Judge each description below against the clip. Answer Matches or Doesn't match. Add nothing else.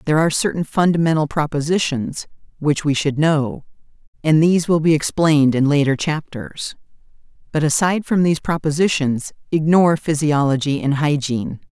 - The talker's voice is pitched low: Doesn't match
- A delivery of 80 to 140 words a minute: Matches